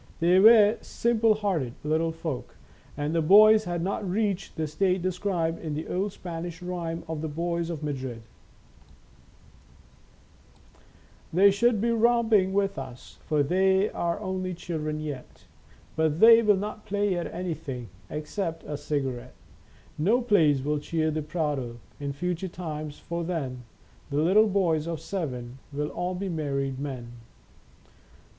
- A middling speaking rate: Yes, average, 145 wpm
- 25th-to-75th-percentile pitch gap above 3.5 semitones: Yes, average, 4.4 semitones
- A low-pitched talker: No, medium, 170 Hz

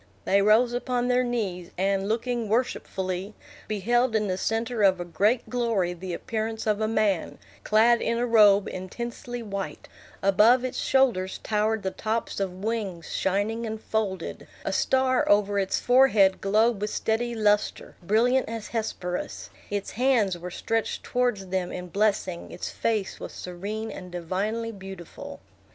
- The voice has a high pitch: Yes, high, 215 Hz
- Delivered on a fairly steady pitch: No, average, 3.3 semitones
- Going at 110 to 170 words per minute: Yes, average, 150 wpm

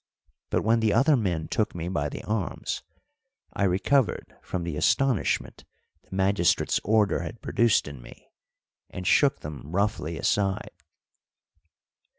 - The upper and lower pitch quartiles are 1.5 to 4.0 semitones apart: No, average, 4.6 semitones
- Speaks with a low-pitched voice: Yes, low, 100 Hz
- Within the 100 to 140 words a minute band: Yes, slow, 135 wpm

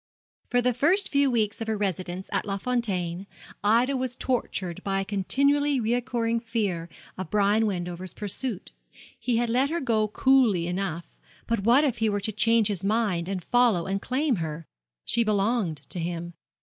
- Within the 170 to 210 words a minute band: Yes, average, 175 wpm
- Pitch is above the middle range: Yes, high, 215 Hz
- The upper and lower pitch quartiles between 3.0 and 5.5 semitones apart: Yes, average, 4.6 semitones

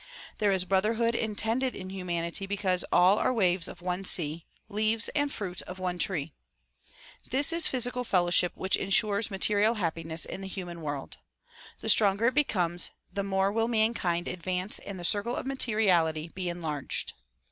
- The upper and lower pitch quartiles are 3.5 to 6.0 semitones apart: Yes, average, 3.8 semitones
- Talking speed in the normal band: Yes, average, 165 wpm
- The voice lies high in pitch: Yes, high, 195 Hz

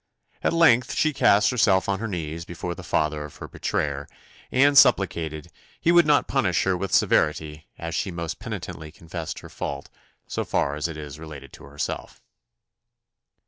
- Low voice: Yes, very low, 85 Hz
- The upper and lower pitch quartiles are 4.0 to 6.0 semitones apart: Yes, average, 5.1 semitones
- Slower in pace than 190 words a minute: Yes, average, 165 wpm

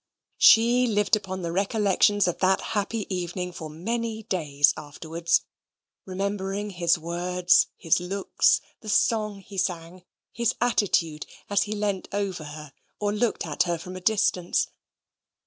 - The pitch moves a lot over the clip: No, average, 3.2 semitones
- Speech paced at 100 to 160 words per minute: Yes, average, 140 wpm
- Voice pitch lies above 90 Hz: Yes, high, 190 Hz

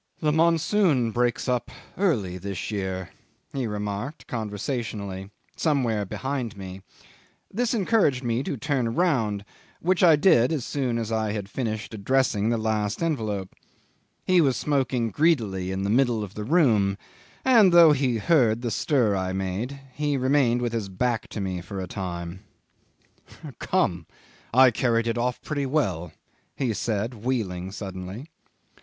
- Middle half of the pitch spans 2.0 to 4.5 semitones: No, wide, 5.5 semitones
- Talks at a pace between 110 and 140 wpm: No, average, 150 wpm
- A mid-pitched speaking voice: No, low, 115 Hz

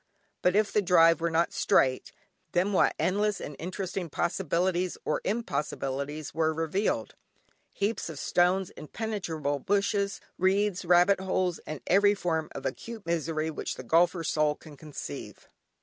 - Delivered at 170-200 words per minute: No, average, 140 wpm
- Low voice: No, medium, 175 Hz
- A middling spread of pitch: Yes, average, 3.9 semitones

